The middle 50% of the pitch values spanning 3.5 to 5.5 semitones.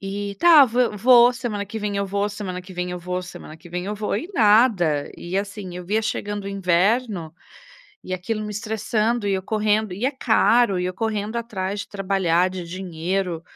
No: average, 3.1 semitones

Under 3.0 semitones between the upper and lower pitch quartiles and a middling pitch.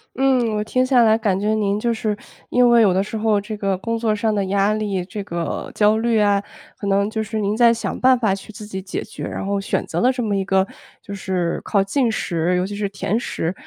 No: narrow, 2.4 semitones; high, 210 Hz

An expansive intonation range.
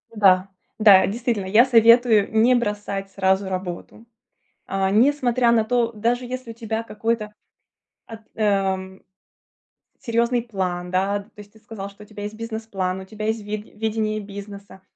No: average, 2.7 semitones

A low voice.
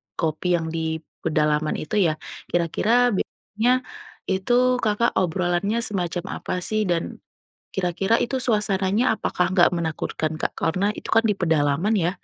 No: medium, 185 Hz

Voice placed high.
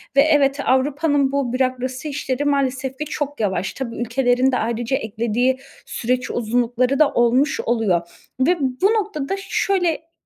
Yes: very high, 260 Hz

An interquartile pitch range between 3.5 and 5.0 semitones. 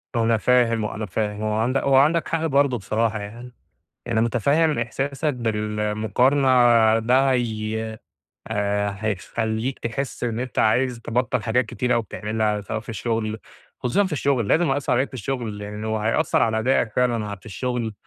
No: average, 2.9 semitones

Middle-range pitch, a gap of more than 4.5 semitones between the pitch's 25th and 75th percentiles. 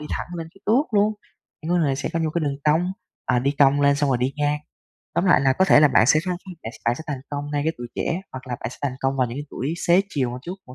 No: medium, 145 Hz; average, 3.9 semitones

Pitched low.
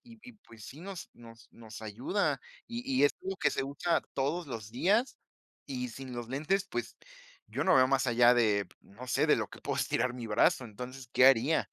Yes: low, 130 Hz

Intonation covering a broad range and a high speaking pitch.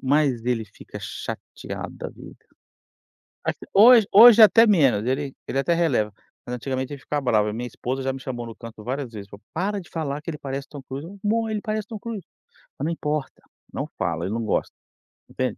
No: wide, 6.4 semitones; low, 135 Hz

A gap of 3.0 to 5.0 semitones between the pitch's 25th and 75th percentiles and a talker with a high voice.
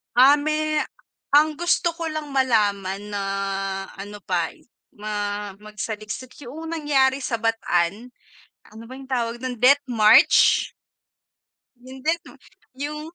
No: wide, 5.6 semitones; very high, 250 Hz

